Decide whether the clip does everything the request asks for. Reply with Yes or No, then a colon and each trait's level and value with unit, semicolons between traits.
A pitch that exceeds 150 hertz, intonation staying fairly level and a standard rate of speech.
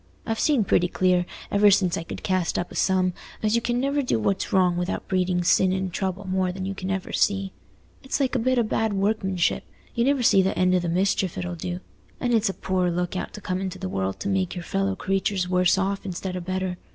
No: high, 190 Hz; narrow, 1.8 semitones; fast, 235 wpm